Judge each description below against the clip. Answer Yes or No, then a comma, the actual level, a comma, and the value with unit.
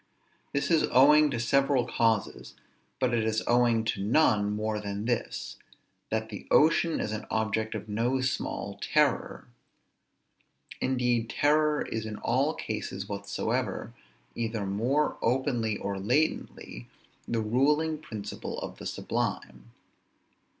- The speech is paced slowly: Yes, slow, 125 wpm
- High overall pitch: No, low, 115 Hz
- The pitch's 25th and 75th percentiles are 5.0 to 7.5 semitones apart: No, average, 3.8 semitones